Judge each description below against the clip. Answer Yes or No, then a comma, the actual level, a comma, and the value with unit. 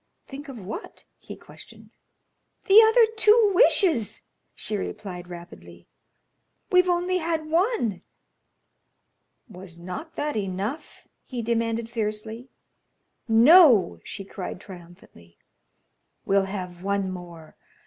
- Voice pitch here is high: Yes, high, 220 Hz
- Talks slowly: Yes, slow, 105 wpm